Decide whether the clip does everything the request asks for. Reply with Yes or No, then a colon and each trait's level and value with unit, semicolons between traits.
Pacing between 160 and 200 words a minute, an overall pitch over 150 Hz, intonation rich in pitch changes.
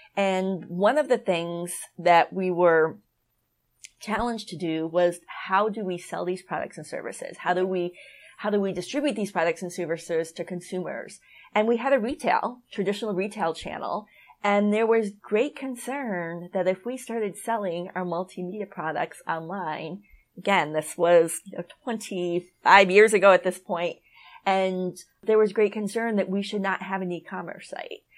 No: average, 170 wpm; high, 190 Hz; average, 3.3 semitones